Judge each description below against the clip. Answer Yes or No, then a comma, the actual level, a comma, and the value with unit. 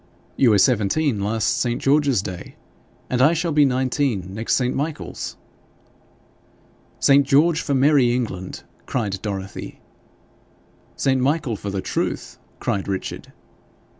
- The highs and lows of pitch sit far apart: Yes, wide, 5.7 semitones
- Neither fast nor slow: No, slow, 125 wpm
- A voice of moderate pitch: No, low, 125 Hz